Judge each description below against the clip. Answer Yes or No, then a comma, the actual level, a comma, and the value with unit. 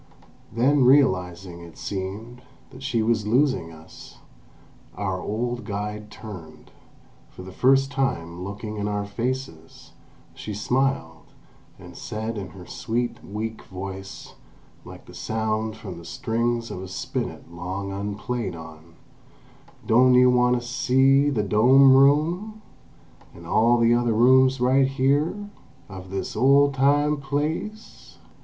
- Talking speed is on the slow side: Yes, slow, 130 wpm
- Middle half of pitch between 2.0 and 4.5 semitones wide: No, average, 5.3 semitones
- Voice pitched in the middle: No, low, 115 Hz